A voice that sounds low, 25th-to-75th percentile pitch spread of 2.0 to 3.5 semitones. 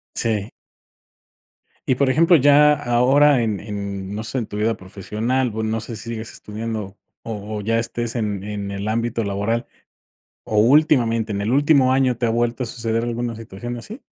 Yes: low, 115 Hz; average, 2.9 semitones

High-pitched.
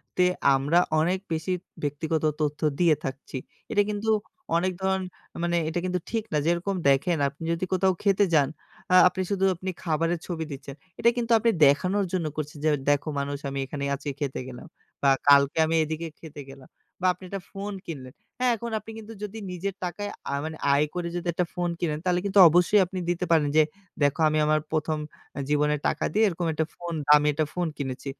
No: medium, 165 Hz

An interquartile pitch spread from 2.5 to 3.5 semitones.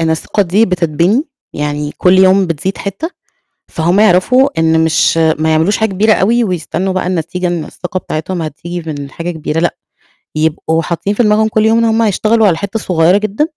No: average, 4.5 semitones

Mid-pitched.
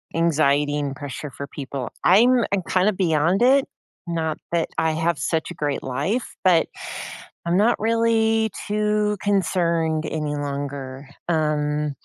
Yes: medium, 165 Hz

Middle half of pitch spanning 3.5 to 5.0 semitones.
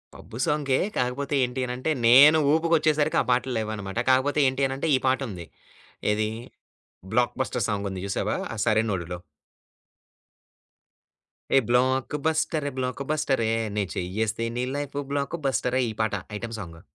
Yes: average, 4.5 semitones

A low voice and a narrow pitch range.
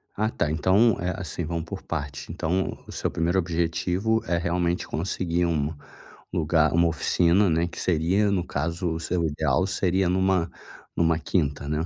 Yes: very low, 85 Hz; narrow, 2.2 semitones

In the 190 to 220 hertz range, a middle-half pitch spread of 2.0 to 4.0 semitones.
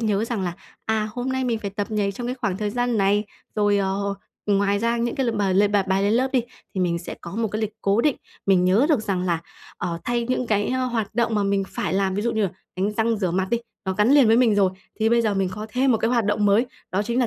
Yes: high, 210 Hz; average, 3.0 semitones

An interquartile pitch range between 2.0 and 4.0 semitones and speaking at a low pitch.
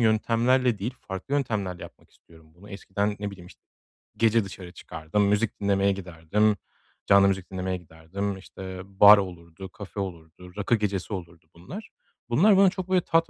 Yes: average, 2.9 semitones; low, 100 Hz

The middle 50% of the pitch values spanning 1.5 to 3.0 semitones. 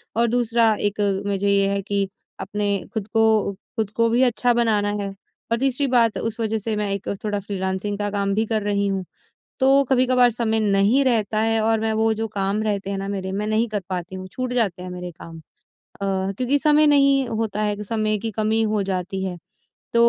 Yes: narrow, 2.5 semitones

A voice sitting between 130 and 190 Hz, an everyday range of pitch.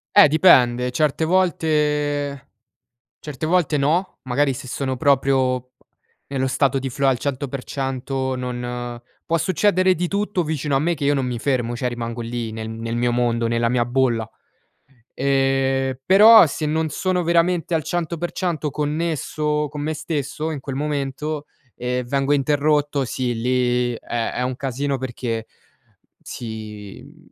Yes: low, 135 Hz; average, 3.6 semitones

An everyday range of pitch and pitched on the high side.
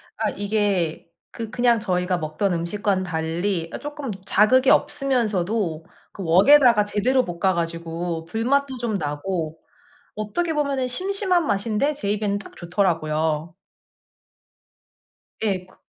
No: wide, 6.2 semitones; high, 200 Hz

